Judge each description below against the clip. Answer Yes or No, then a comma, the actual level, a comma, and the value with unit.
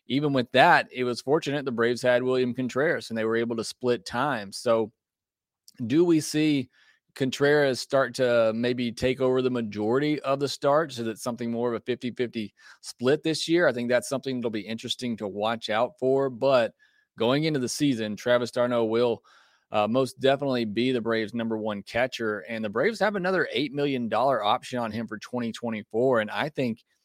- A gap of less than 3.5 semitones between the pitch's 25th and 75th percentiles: Yes, average, 2.9 semitones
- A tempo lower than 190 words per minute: No, average, 195 wpm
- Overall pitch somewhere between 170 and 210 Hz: No, low, 125 Hz